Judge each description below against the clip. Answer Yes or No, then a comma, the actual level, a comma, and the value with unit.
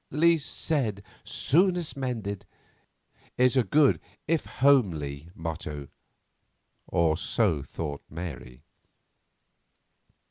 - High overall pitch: No, low, 100 Hz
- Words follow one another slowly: Yes, slow, 85 wpm